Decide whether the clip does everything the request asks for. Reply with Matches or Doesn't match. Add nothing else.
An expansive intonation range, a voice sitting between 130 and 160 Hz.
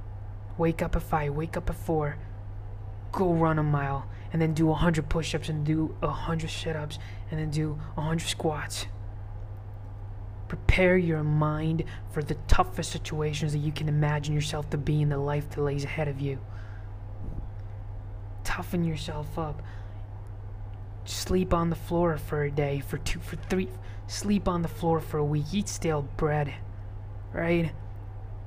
Matches